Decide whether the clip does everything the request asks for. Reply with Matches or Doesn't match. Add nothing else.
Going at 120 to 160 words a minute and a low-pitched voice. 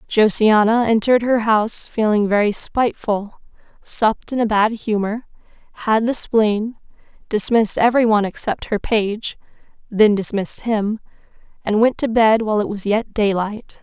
Doesn't match